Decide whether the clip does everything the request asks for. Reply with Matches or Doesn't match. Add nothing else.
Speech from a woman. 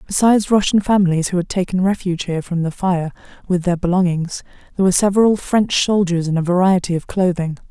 Matches